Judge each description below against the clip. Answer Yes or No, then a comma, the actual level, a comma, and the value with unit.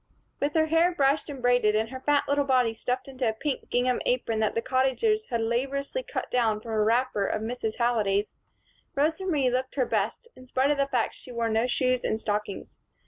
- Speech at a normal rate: No, fast, 215 wpm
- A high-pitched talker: Yes, very high, 250 Hz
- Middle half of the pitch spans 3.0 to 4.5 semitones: Yes, average, 3.6 semitones